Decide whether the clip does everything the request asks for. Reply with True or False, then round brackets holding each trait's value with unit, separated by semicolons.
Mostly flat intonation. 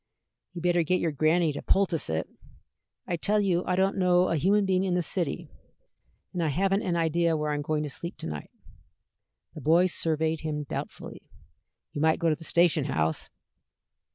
False (3.0 semitones)